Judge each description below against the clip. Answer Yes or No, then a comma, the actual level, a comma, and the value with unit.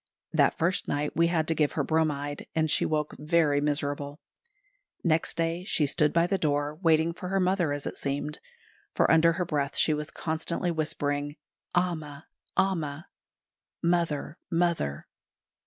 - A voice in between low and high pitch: Yes, medium, 155 Hz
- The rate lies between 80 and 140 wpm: No, average, 155 wpm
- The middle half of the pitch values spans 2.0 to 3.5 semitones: Yes, narrow, 2.5 semitones